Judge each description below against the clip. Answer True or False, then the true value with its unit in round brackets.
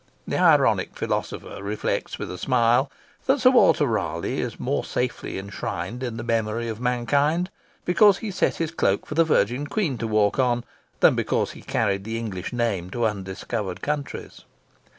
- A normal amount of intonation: False (5.8 semitones)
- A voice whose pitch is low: True (120 Hz)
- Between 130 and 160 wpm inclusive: False (170 wpm)